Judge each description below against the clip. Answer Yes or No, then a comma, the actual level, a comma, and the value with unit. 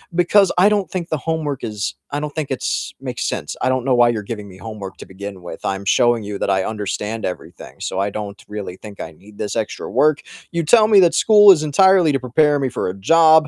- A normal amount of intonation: No, wide, 7.8 semitones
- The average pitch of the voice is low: Yes, low, 125 Hz